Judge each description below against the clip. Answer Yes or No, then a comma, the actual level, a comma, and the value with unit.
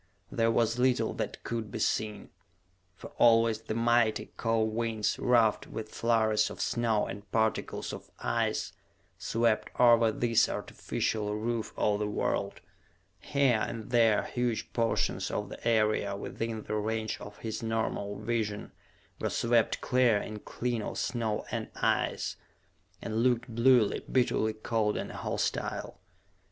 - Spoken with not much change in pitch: Yes, narrow, 1.5 semitones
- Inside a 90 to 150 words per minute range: Yes, average, 140 wpm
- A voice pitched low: Yes, low, 115 Hz